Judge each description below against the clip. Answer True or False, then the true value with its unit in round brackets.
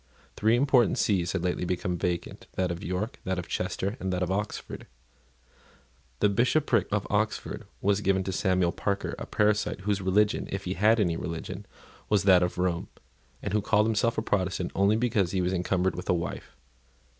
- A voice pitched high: False (95 Hz)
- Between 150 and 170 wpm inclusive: False (185 wpm)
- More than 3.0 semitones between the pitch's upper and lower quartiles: False (2.6 semitones)